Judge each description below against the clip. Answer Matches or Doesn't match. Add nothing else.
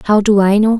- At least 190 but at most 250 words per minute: Doesn't match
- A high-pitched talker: Matches